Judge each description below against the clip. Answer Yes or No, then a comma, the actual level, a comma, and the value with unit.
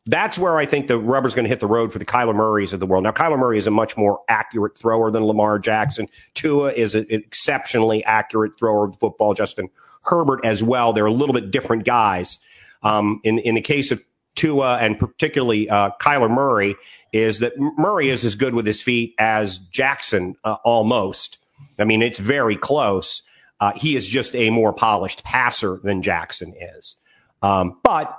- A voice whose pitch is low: Yes, low, 110 Hz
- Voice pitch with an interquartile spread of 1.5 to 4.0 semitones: Yes, average, 2.8 semitones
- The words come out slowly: No, average, 200 wpm